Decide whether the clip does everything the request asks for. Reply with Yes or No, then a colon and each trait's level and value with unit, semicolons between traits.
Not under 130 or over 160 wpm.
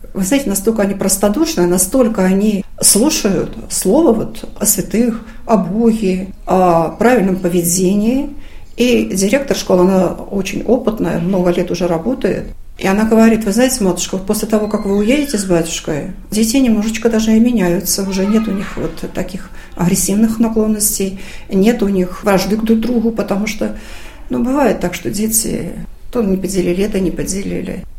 Yes: average, 155 wpm